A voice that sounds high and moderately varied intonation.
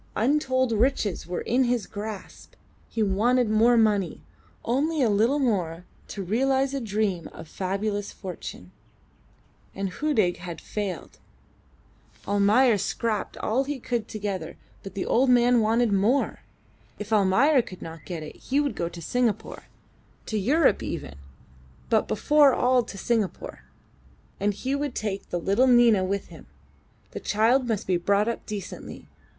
Yes: high, 215 Hz; average, 4.2 semitones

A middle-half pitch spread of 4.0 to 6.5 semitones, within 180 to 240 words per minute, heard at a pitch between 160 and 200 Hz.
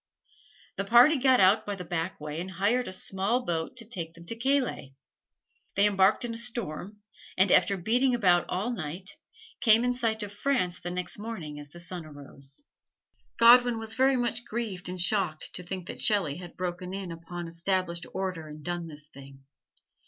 Yes: average, 5.2 semitones; average, 185 wpm; high, 190 Hz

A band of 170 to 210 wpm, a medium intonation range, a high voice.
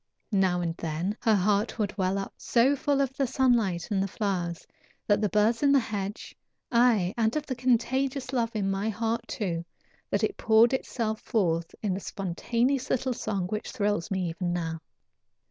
Yes: average, 180 wpm; average, 4.1 semitones; high, 215 Hz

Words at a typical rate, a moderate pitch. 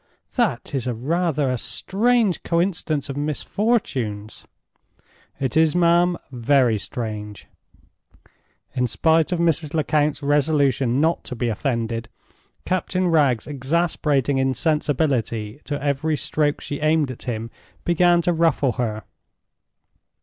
No: slow, 115 wpm; medium, 145 Hz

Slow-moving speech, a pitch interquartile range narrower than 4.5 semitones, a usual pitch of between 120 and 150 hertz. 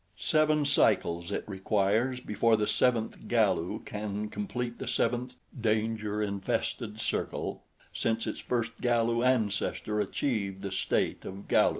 No: slow, 125 wpm; average, 2.9 semitones; low, 110 Hz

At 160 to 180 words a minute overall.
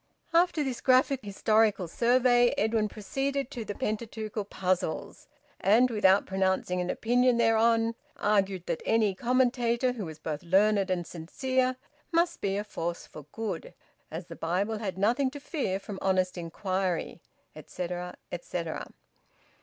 No: average, 140 wpm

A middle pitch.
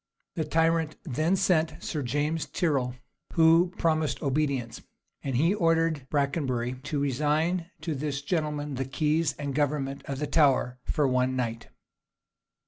Yes: medium, 150 Hz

